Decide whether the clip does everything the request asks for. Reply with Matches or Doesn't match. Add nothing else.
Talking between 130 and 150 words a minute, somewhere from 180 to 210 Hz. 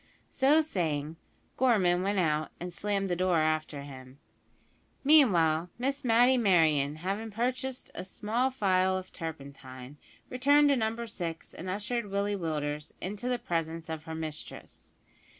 Matches